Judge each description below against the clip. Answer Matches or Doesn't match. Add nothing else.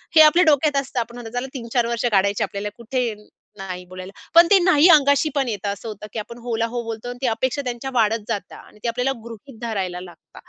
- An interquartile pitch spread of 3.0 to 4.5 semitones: Matches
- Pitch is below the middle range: Doesn't match